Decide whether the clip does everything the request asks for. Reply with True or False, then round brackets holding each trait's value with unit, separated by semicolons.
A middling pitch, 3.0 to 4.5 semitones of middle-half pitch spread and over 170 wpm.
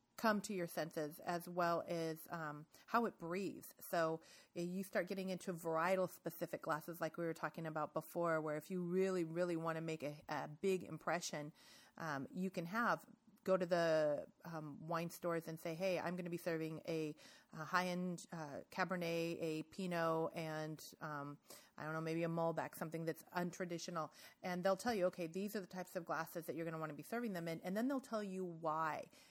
False (170 Hz; 2.5 semitones; 205 wpm)